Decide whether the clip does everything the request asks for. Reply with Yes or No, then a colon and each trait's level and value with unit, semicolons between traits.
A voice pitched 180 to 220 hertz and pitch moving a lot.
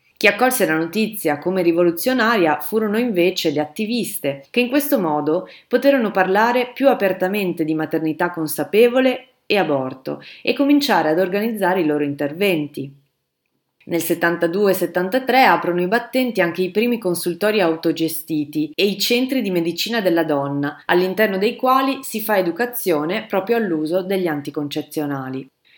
Yes: medium, 185 Hz; wide, 6.0 semitones